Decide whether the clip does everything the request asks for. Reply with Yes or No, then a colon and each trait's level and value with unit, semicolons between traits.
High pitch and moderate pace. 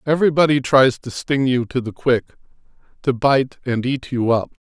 No: low, 130 Hz; average, 180 wpm